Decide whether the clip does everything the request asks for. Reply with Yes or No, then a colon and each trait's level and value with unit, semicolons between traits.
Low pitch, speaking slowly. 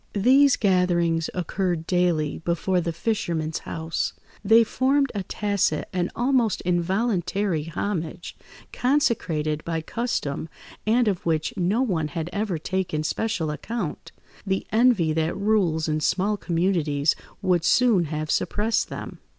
No: medium, 180 Hz; slow, 125 wpm